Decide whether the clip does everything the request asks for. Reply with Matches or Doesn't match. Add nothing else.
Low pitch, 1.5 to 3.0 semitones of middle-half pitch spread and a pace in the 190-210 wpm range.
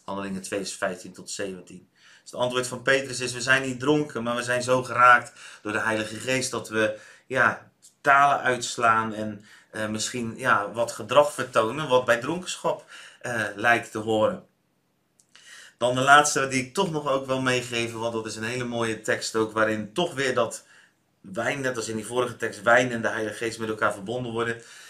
Matches